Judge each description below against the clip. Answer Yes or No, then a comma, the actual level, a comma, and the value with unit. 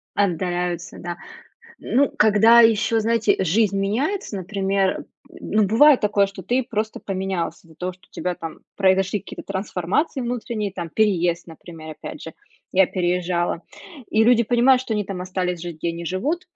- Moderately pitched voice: No, high, 195 Hz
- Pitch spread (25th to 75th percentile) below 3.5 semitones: No, average, 3.9 semitones